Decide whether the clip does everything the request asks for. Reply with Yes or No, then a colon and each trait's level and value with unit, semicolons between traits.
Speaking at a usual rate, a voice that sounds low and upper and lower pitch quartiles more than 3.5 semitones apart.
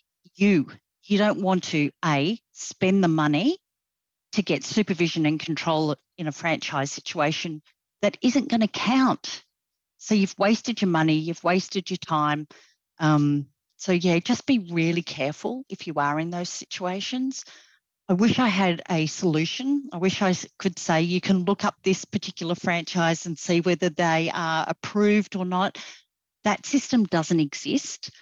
No: average, 160 wpm; medium, 180 Hz; average, 4.3 semitones